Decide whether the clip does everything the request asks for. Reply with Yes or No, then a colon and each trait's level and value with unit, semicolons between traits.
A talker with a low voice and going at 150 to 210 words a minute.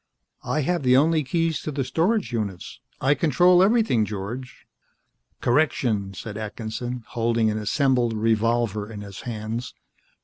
No: low, 120 Hz; slow, 135 wpm